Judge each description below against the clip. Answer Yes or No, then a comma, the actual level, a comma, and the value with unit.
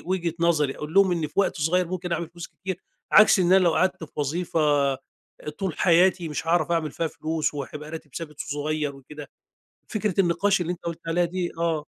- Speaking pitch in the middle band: Yes, medium, 170 Hz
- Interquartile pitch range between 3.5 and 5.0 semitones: No, average, 2.8 semitones